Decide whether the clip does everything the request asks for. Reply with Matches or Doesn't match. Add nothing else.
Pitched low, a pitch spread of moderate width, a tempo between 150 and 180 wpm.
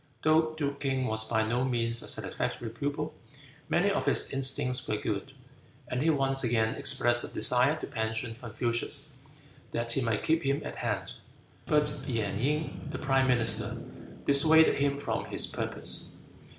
Matches